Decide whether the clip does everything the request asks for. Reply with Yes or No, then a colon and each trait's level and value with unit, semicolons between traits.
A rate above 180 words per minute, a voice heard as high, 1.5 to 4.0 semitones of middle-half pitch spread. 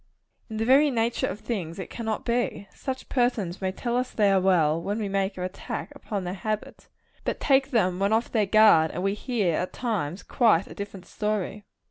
Yes: fast, 205 wpm; high, 205 Hz; average, 3.7 semitones